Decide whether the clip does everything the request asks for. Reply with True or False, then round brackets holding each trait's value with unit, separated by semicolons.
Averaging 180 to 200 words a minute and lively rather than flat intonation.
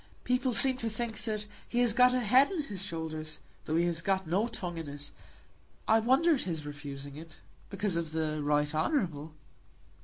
True (190 wpm; 7.1 semitones)